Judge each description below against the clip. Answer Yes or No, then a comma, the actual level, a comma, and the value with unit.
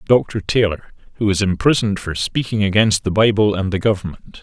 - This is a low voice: Yes, low, 100 Hz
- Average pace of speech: Yes, average, 175 wpm